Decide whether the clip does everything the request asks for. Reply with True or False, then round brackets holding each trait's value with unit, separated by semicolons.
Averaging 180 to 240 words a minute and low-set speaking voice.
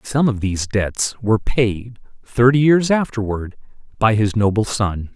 False (150 wpm; 115 Hz)